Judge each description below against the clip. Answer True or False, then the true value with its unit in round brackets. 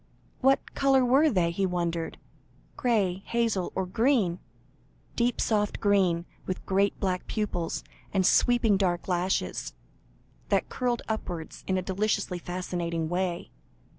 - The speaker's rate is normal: False (125 wpm)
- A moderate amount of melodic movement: True (4.2 semitones)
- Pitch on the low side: False (190 Hz)